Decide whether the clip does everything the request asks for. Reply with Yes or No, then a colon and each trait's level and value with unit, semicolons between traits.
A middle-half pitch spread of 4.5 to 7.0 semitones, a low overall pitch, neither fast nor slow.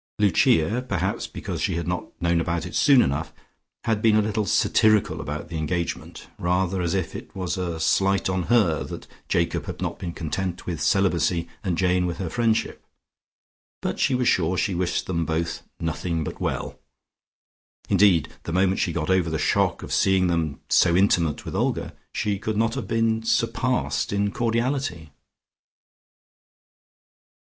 No: average, 3.9 semitones; very low, 90 Hz; average, 165 wpm